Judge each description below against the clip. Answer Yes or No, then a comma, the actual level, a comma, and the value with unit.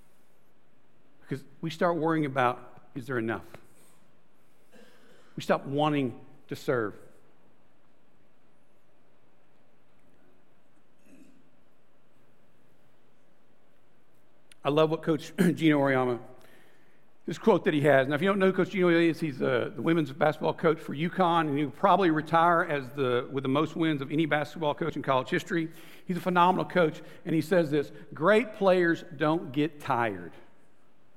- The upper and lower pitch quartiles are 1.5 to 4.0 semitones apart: Yes, average, 3.5 semitones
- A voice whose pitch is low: No, medium, 155 Hz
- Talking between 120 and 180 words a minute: Yes, average, 140 wpm